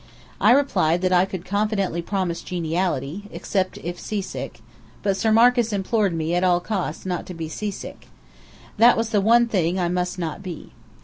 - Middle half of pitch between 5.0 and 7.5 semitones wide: No, average, 3.3 semitones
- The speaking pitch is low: No, medium, 185 Hz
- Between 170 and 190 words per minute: Yes, average, 175 wpm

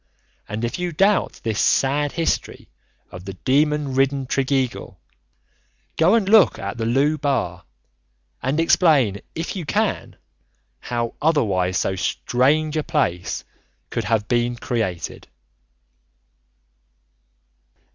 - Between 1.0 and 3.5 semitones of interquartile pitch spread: No, wide, 5.6 semitones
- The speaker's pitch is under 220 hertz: Yes, low, 135 Hz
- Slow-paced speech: Yes, slow, 115 wpm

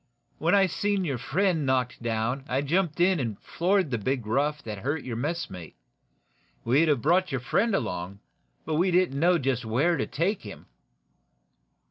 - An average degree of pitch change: No, wide, 6.3 semitones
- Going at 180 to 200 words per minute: No, average, 170 wpm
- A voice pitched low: No, medium, 145 Hz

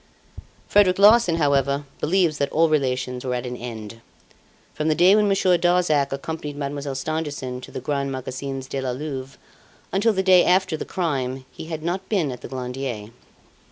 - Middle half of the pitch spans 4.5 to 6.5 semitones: Yes, average, 5.0 semitones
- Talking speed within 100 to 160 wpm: No, average, 175 wpm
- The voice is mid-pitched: Yes, medium, 145 Hz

